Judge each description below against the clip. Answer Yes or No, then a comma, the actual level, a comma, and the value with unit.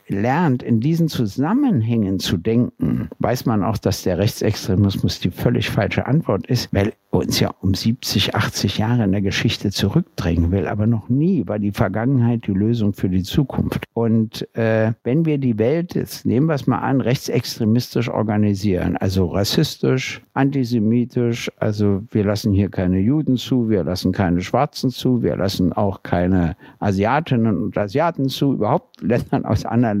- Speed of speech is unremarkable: Yes, average, 165 wpm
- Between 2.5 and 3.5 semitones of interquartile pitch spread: No, average, 4.2 semitones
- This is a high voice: No, low, 110 Hz